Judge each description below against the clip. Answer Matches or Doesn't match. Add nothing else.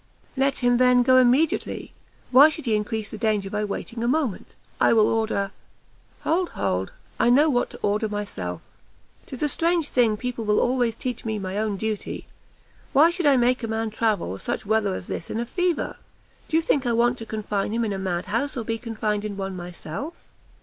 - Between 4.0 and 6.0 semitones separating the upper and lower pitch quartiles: Doesn't match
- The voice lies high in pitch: Matches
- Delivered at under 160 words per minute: Doesn't match